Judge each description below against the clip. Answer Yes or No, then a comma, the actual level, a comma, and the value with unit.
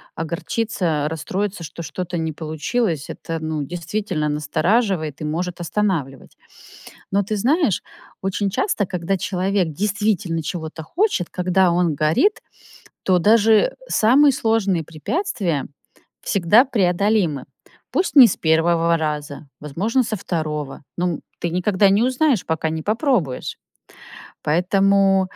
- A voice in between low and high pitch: Yes, medium, 180 Hz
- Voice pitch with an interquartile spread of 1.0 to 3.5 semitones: No, average, 4.7 semitones